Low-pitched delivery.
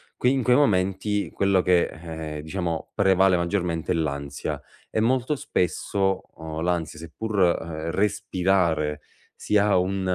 Yes: very low, 90 Hz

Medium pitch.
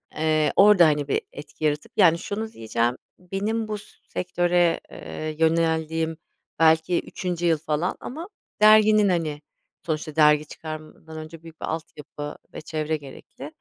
Yes: medium, 160 Hz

